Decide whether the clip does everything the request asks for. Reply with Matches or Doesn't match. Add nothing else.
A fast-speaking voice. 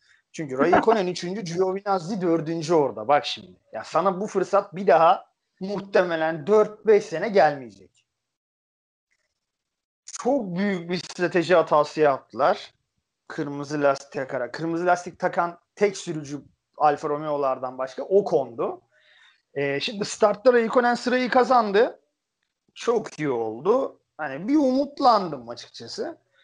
Doesn't match